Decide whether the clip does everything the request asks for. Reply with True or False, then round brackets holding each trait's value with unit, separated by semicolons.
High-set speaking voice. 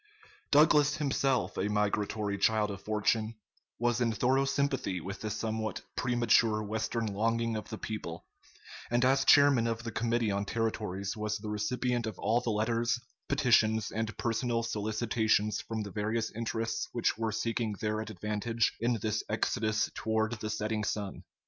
False (110 Hz)